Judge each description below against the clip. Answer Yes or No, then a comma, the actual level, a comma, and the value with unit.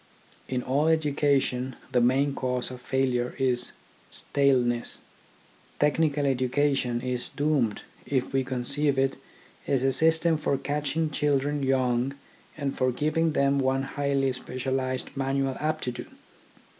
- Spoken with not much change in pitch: Yes, narrow, 2.1 semitones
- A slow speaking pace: Yes, slow, 120 wpm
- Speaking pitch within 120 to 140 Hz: Yes, low, 135 Hz